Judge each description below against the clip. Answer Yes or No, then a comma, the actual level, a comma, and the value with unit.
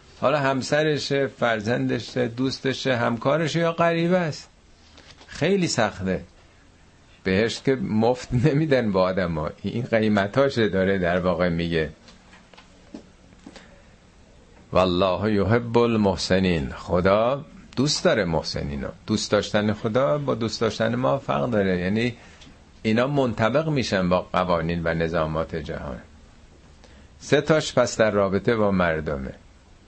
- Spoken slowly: No, average, 115 wpm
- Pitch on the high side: No, low, 105 Hz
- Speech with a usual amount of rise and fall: No, wide, 6.3 semitones